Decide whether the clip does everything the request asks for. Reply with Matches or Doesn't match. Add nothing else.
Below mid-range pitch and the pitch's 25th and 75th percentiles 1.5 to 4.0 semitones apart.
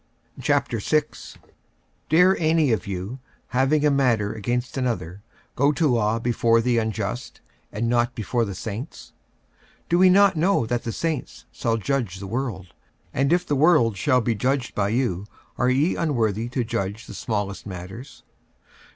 Doesn't match